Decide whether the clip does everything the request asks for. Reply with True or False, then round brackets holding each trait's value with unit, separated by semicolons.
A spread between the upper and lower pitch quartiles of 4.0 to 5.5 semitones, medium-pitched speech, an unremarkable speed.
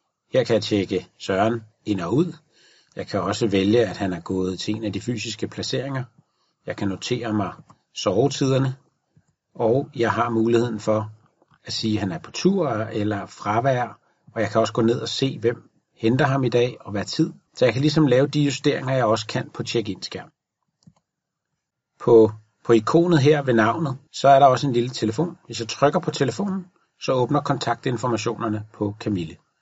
False (4.4 semitones; 120 Hz; 190 wpm)